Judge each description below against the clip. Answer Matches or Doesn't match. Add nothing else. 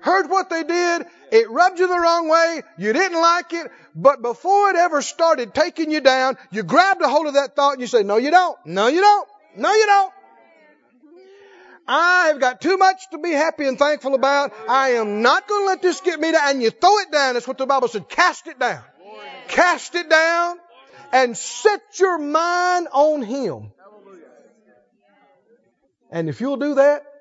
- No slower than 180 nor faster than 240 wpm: Matches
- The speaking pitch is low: Doesn't match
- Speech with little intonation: Doesn't match